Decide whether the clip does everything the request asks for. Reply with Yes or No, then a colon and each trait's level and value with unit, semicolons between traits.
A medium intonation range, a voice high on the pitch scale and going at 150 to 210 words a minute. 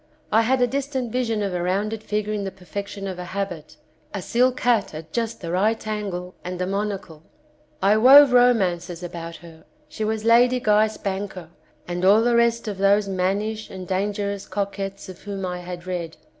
Yes: average, 3.3 semitones; high, 200 Hz; average, 185 wpm